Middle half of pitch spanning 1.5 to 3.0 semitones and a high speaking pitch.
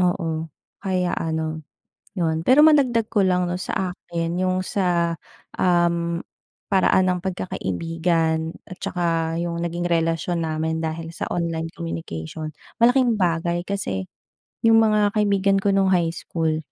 No: narrow, 2.5 semitones; medium, 175 Hz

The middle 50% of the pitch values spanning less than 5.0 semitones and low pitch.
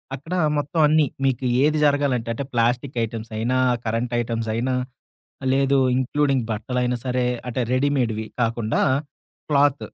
Yes: average, 3.3 semitones; low, 125 Hz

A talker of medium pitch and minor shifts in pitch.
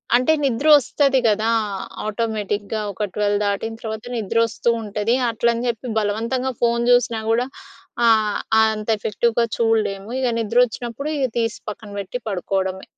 No: high, 225 Hz; narrow, 2.2 semitones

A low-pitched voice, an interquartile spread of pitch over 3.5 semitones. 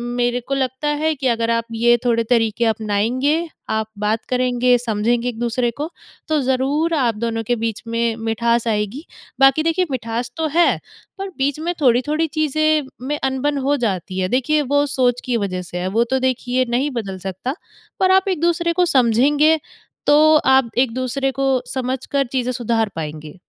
No: very high, 250 Hz; average, 4.0 semitones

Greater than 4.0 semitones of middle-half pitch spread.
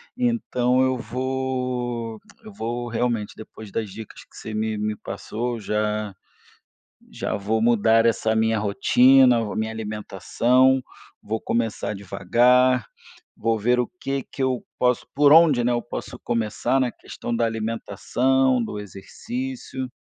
No: average, 2.8 semitones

